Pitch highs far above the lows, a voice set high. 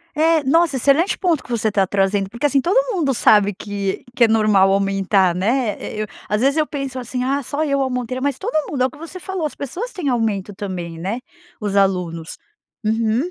Yes: wide, 6.2 semitones; high, 235 Hz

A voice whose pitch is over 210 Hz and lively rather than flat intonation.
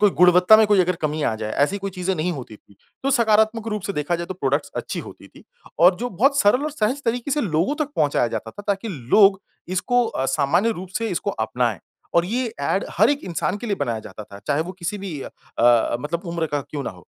No: medium, 185 Hz; wide, 6.6 semitones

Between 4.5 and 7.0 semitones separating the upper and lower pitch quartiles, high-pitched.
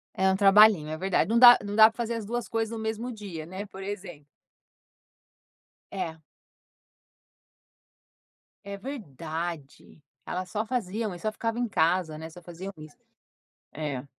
Yes: average, 5.0 semitones; high, 195 Hz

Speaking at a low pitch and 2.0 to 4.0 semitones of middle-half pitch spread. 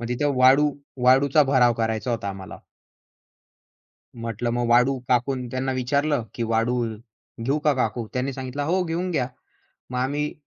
Yes: low, 130 Hz; average, 2.8 semitones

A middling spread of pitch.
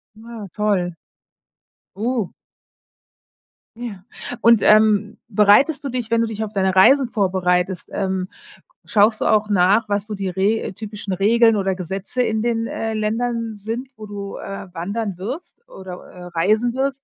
Yes: average, 3.0 semitones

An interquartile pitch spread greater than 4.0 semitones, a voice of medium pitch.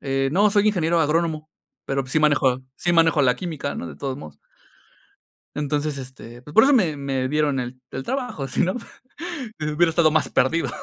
No: average, 3.7 semitones; medium, 150 Hz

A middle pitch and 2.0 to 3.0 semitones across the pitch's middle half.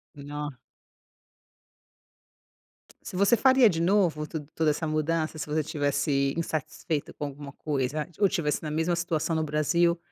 Yes: medium, 155 Hz; narrow, 2.4 semitones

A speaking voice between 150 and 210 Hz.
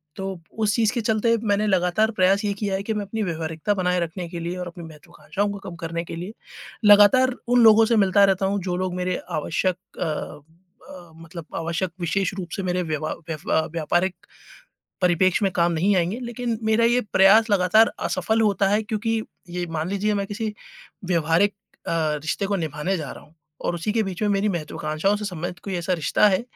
Yes: high, 190 Hz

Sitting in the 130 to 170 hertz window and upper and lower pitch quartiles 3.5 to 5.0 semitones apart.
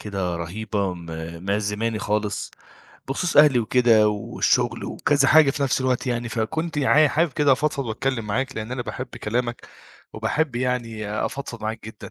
No: low, 120 Hz; average, 4.2 semitones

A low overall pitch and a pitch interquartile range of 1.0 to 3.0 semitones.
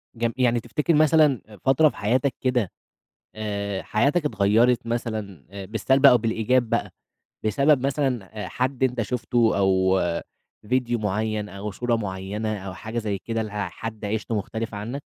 No: low, 115 Hz; average, 3.4 semitones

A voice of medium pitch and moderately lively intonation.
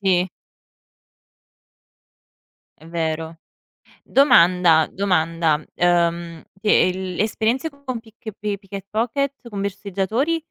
No: high, 195 Hz; average, 4.7 semitones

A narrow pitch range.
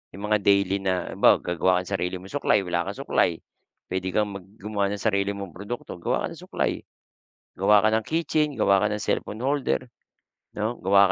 Yes: narrow, 2.2 semitones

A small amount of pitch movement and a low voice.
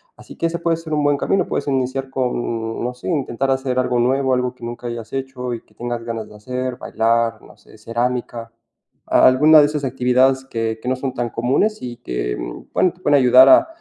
Yes: narrow, 2.3 semitones; low, 125 Hz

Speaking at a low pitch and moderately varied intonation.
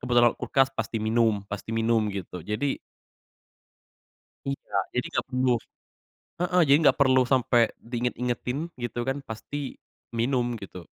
Yes: low, 120 Hz; average, 3.0 semitones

